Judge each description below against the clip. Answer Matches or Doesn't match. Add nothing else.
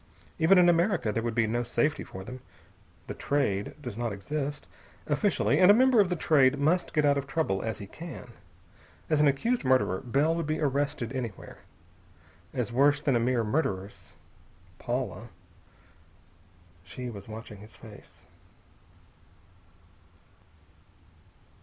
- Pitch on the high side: Doesn't match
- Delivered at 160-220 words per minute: Doesn't match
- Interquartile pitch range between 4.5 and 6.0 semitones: Matches